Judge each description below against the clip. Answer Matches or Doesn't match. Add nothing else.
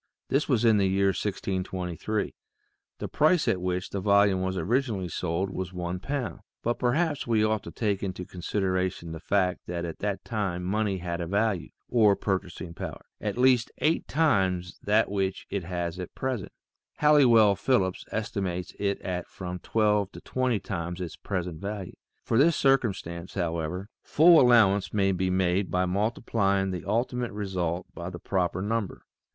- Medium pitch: Doesn't match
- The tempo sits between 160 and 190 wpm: Matches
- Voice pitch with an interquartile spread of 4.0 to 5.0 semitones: Doesn't match